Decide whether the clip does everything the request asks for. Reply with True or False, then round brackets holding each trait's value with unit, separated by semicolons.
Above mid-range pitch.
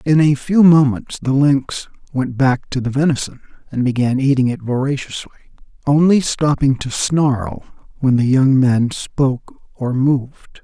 False (135 Hz)